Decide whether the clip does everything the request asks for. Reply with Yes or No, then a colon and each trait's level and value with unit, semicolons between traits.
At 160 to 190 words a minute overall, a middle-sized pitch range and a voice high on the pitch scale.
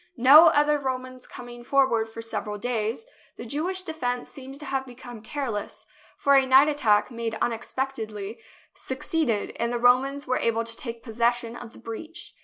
Yes: average, 165 wpm; average, 3.1 semitones; high, 245 Hz